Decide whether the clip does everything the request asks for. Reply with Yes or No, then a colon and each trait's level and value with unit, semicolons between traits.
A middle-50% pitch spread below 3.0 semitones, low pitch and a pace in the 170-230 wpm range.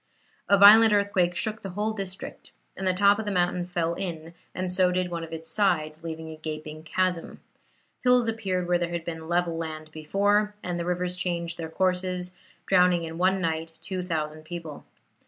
No: narrow, 2.6 semitones; medium, 180 Hz; average, 185 wpm